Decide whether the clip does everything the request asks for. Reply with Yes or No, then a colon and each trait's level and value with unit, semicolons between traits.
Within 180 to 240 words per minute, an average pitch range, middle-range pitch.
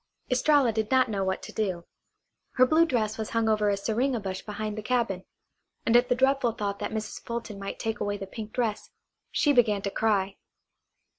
No: average, 200 wpm; average, 3.2 semitones; high, 220 Hz